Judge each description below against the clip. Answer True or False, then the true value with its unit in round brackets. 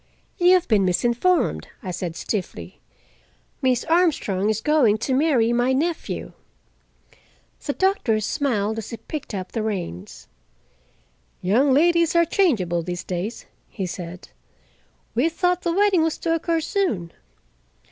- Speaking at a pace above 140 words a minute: False (135 wpm)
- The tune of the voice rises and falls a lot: True (9.0 semitones)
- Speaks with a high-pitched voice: True (245 Hz)